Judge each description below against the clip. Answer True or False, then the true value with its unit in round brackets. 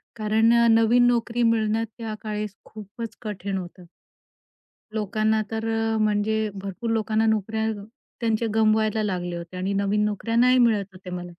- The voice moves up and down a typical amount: False (1.9 semitones)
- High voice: True (215 Hz)